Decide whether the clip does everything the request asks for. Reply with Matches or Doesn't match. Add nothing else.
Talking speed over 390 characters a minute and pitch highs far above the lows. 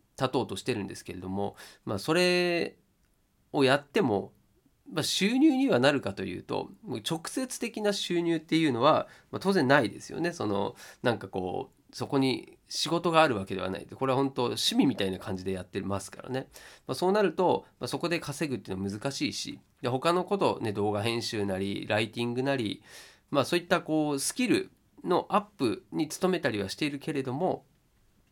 Doesn't match